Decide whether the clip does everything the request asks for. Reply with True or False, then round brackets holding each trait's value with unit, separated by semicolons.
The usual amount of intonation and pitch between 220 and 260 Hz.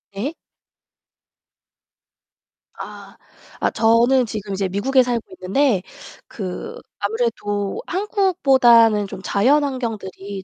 True (4.7 semitones; 225 Hz)